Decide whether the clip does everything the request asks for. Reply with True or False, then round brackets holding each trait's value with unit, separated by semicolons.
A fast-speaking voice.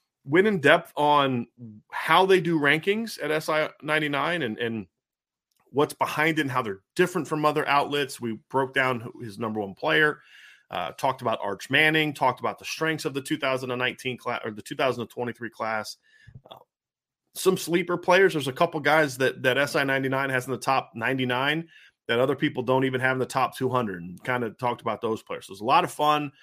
True (225 wpm)